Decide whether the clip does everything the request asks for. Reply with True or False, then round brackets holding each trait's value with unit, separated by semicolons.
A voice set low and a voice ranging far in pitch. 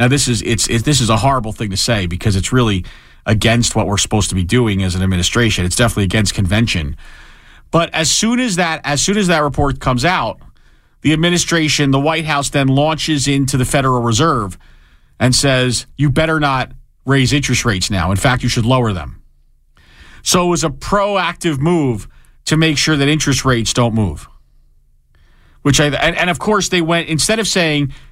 True (130 Hz; 6.0 semitones)